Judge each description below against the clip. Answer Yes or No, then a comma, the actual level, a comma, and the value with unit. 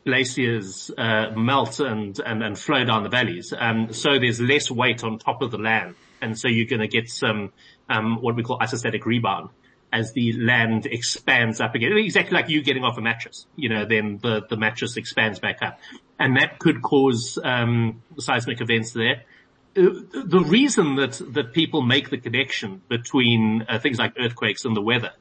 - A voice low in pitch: Yes, low, 115 Hz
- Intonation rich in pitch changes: No, average, 3.5 semitones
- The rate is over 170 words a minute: Yes, average, 190 wpm